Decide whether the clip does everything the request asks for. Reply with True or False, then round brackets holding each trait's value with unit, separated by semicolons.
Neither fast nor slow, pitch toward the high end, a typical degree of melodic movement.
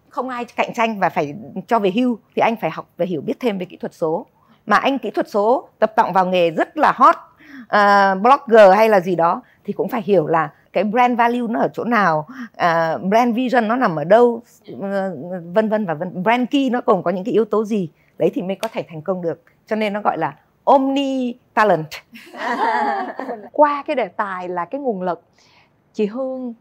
True (220 wpm; 220 Hz; 4.9 semitones)